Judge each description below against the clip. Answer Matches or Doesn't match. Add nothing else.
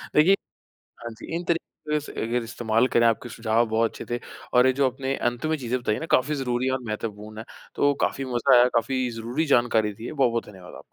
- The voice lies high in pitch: Doesn't match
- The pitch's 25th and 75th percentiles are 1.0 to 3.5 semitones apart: Matches